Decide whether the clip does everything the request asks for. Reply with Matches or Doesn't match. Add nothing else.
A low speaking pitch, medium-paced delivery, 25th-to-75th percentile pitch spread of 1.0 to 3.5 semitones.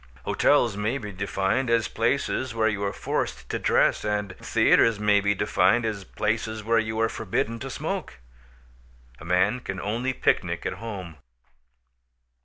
Matches